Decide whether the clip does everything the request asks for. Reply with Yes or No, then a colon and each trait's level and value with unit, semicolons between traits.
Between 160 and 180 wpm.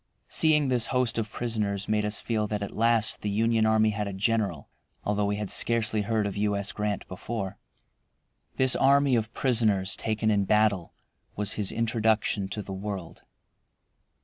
Yes: average, 170 wpm